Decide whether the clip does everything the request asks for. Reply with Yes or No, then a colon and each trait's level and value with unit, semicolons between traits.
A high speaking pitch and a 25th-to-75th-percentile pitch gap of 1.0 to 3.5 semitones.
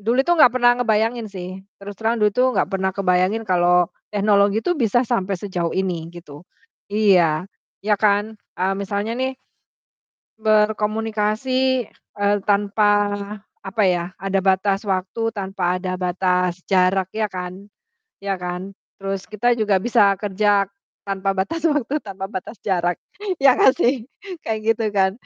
Yes: high, 200 Hz; average, 2.8 semitones